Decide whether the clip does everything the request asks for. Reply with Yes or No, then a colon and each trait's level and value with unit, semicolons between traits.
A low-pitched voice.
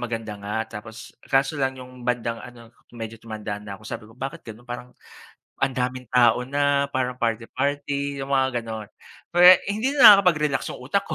Yes: low, 125 Hz